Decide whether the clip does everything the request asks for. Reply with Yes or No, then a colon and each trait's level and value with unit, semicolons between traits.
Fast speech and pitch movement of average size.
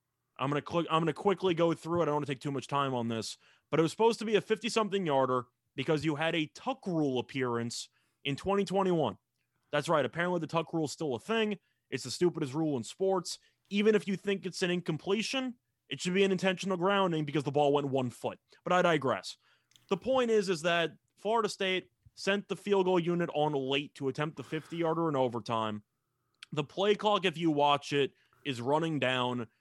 No: fast, 220 wpm; wide, 5.7 semitones